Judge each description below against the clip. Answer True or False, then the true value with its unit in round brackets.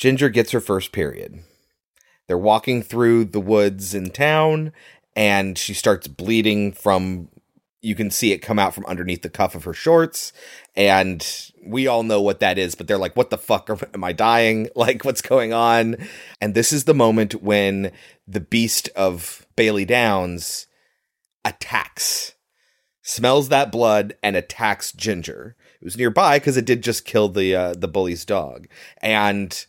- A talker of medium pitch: False (105 Hz)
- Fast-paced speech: False (165 wpm)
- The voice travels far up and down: False (3.2 semitones)